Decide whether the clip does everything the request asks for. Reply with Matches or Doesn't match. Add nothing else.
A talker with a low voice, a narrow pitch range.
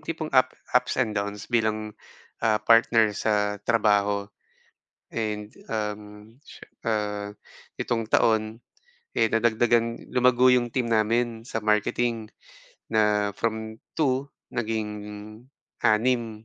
Matches